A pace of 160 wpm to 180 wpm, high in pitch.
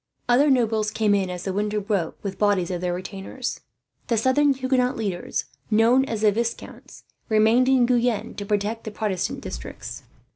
Yes: average, 170 wpm; high, 220 Hz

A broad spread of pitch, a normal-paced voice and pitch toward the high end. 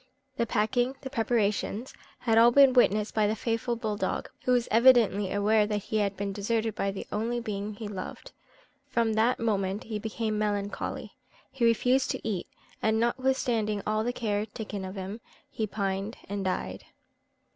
No: narrow, 2.4 semitones; average, 170 wpm; high, 220 Hz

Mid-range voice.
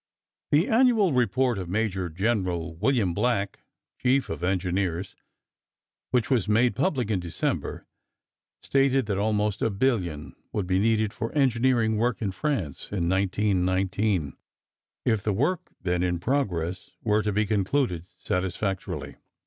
No: low, 105 Hz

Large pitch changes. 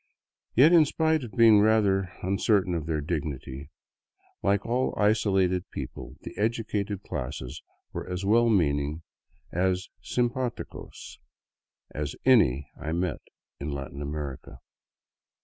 Yes: wide, 6.5 semitones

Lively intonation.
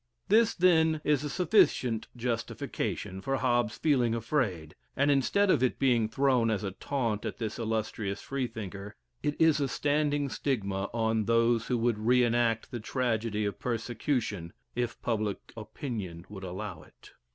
No: average, 4.2 semitones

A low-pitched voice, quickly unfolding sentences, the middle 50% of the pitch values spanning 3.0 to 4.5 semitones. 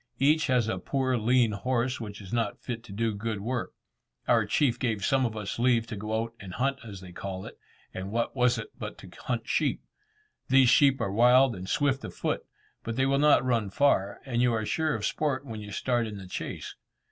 Yes: low, 120 Hz; fast, 225 wpm; average, 3.5 semitones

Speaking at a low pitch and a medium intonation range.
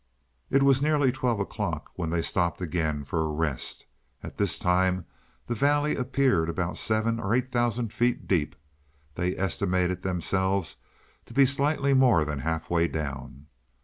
No: very low, 95 Hz; wide, 7.1 semitones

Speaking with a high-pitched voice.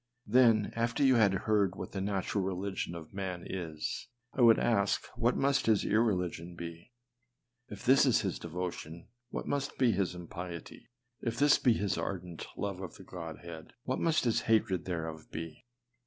No: very low, 95 Hz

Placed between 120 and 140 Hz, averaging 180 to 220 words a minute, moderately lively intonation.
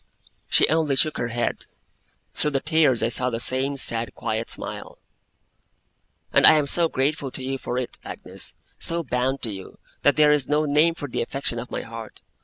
Yes: low, 135 Hz; average, 195 wpm; average, 3.7 semitones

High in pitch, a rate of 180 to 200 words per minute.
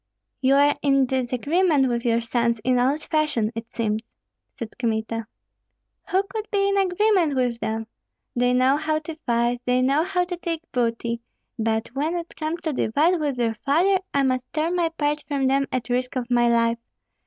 Yes: very high, 265 Hz; average, 185 wpm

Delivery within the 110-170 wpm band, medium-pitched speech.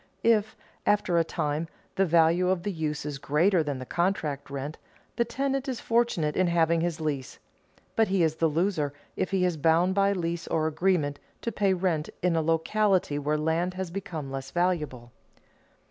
No: average, 180 wpm; medium, 170 Hz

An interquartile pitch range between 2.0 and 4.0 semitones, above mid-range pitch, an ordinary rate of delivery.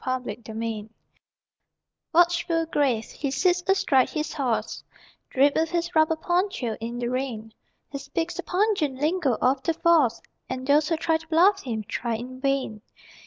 No: average, 5.2 semitones; very high, 280 Hz; average, 160 wpm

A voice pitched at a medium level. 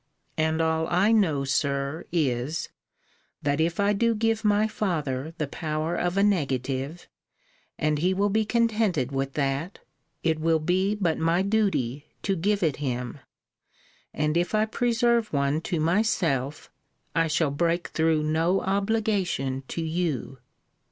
Yes: medium, 165 Hz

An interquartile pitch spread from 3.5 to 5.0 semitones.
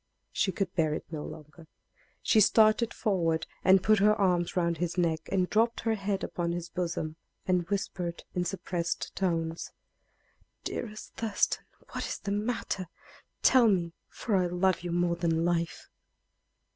No: average, 3.1 semitones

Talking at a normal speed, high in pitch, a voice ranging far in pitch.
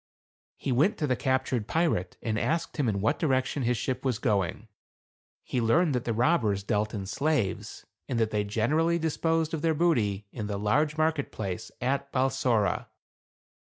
No: average, 170 wpm; low, 130 Hz; wide, 6.3 semitones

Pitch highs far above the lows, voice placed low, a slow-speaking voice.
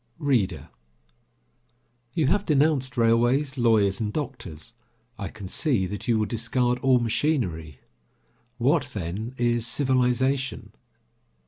No: average, 4.0 semitones; low, 120 Hz; slow, 110 wpm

